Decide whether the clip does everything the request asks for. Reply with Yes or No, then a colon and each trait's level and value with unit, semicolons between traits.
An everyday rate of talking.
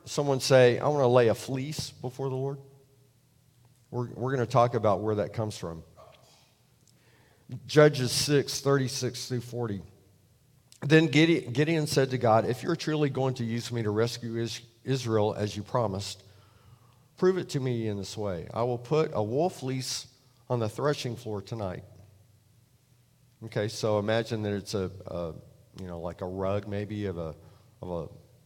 Yes: average, 165 wpm